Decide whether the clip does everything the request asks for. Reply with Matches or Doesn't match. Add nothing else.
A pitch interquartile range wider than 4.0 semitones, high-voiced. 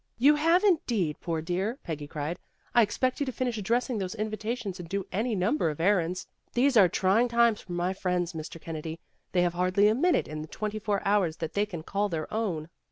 Matches